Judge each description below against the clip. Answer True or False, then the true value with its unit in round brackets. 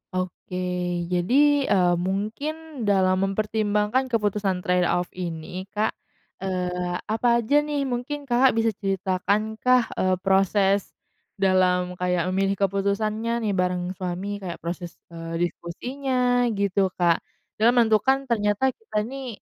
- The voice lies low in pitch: False (200 Hz)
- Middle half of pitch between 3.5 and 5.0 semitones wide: True (3.9 semitones)